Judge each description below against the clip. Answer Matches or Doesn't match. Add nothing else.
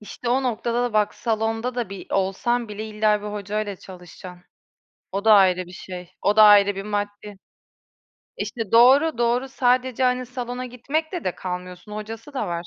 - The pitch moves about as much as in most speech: Matches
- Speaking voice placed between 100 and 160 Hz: Doesn't match